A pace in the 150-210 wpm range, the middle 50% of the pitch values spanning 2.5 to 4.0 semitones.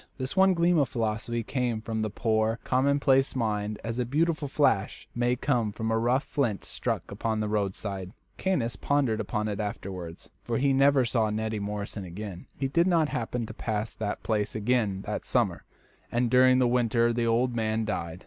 Yes: average, 185 wpm; average, 3.3 semitones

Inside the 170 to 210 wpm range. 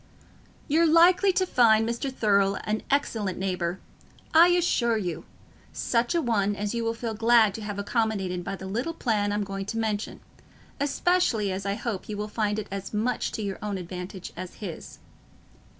Yes: average, 175 wpm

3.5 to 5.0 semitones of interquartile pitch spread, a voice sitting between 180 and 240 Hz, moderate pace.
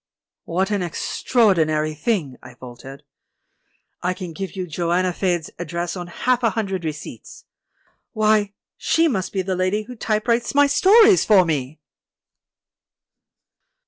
No: average, 4.5 semitones; medium, 185 Hz; slow, 130 wpm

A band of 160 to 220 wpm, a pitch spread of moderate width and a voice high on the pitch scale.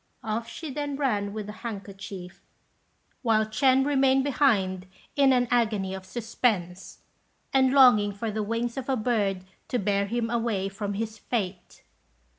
No: average, 150 wpm; average, 4.1 semitones; high, 220 Hz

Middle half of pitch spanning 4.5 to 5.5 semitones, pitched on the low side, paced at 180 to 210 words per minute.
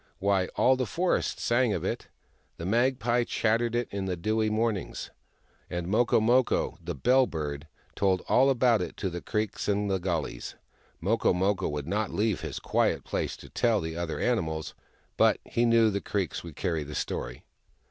Yes: average, 5.1 semitones; low, 105 Hz; average, 185 wpm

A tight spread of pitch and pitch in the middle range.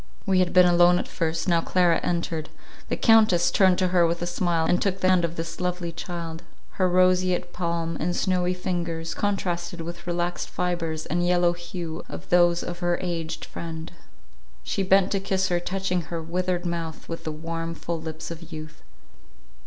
Yes: narrow, 1.5 semitones; medium, 175 Hz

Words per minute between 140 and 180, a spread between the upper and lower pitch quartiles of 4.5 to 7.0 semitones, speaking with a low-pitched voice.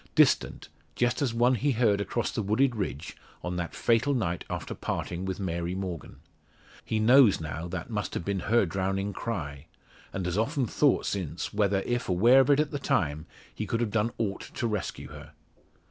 No: average, 190 wpm; average, 4.9 semitones; low, 105 Hz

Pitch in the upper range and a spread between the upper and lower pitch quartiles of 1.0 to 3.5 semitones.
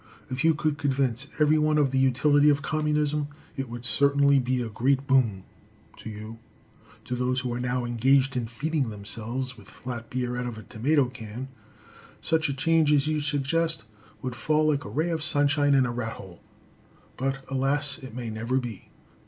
No: low, 135 Hz; average, 3.2 semitones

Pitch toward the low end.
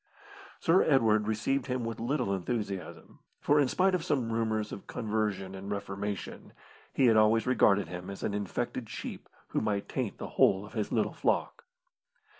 Yes: low, 110 Hz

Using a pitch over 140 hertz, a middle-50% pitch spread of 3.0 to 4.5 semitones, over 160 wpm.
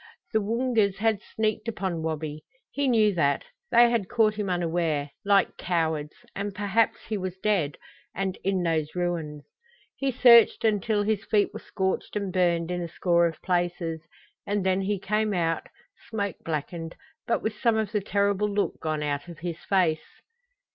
Yes: high, 190 Hz; average, 4.1 semitones; average, 170 wpm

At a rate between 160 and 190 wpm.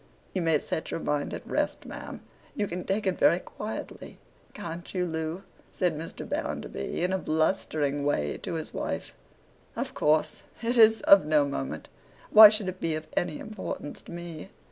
Yes: average, 170 wpm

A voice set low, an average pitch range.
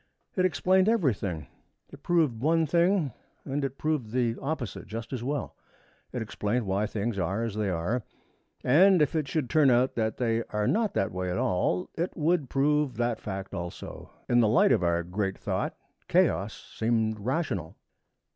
No: low, 120 Hz; wide, 6.3 semitones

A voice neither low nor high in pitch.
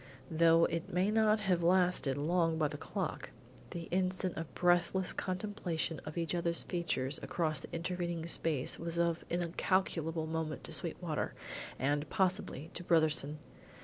Yes: medium, 170 Hz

